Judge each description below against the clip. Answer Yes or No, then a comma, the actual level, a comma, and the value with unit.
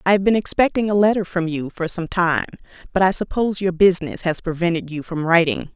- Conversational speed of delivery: No, fast, 220 wpm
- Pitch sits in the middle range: Yes, medium, 180 Hz